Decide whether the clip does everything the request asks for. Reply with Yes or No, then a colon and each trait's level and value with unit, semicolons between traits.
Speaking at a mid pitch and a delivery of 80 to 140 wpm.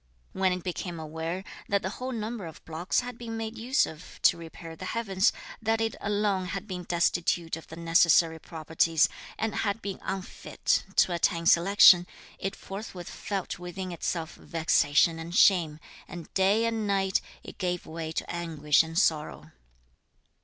No: medium, 180 Hz; average, 160 wpm